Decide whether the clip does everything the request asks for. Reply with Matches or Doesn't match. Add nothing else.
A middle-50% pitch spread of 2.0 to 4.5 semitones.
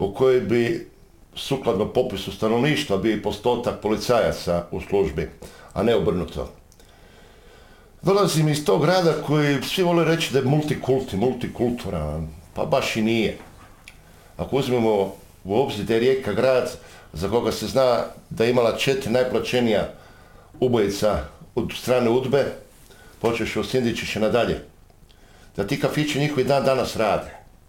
Doesn't match